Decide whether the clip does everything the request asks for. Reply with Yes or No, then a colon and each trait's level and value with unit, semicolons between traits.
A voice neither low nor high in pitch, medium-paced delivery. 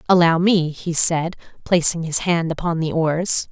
Yes: medium, 165 Hz; average, 170 wpm